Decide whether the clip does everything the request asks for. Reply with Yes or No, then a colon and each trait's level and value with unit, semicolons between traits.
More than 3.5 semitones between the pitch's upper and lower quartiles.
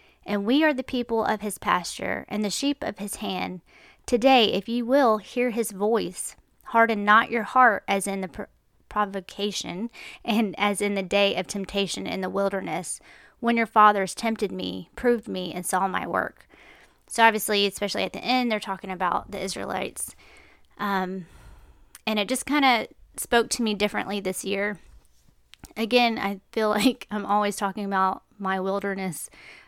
No: average, 2.9 semitones